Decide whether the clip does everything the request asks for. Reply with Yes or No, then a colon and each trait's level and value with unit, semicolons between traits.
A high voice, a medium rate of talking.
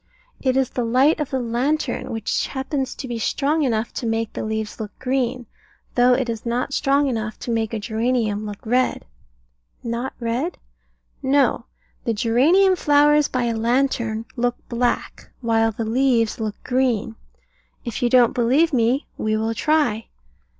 Yes: high, 240 Hz; average, 160 wpm